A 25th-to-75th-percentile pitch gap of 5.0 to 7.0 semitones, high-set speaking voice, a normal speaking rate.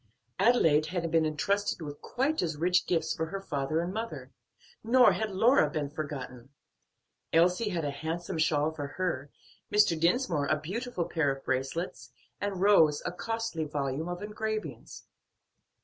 No: average, 5.3 semitones; medium, 165 Hz; average, 150 wpm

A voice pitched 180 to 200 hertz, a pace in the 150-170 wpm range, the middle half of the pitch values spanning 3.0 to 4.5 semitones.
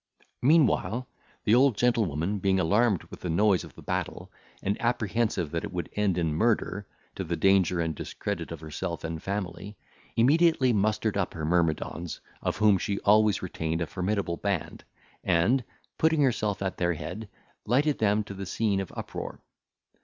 No: low, 100 Hz; average, 165 wpm; average, 4.1 semitones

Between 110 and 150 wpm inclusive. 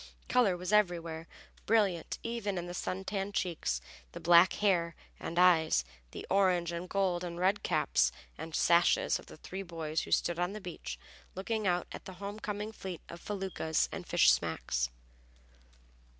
No: average, 165 wpm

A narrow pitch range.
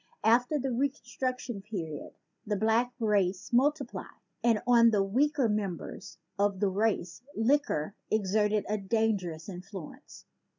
No: average, 3.8 semitones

